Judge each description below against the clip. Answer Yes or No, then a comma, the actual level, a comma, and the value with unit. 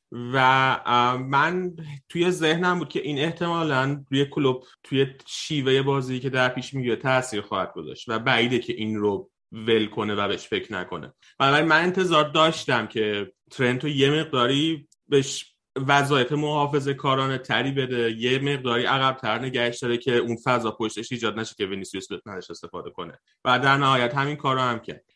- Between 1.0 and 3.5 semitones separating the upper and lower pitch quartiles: Yes, average, 3.0 semitones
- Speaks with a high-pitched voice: No, low, 130 Hz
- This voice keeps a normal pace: No, fast, 165 wpm